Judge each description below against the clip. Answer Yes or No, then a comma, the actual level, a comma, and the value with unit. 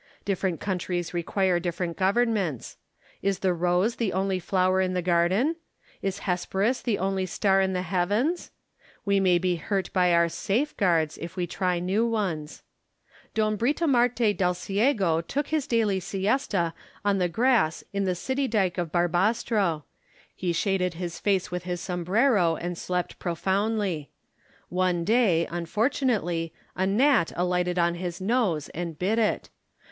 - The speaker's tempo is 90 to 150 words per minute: Yes, average, 145 wpm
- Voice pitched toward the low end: No, medium, 185 Hz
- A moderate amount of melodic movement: Yes, average, 3.3 semitones